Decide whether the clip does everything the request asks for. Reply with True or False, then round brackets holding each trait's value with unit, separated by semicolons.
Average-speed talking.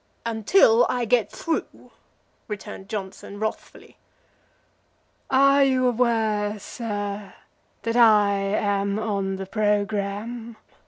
False (95 wpm)